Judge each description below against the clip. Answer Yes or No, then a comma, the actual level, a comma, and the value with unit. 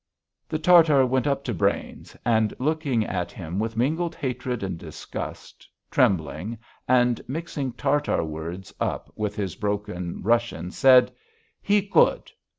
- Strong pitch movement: Yes, wide, 6.2 semitones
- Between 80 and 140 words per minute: Yes, slow, 135 wpm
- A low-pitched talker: Yes, low, 120 Hz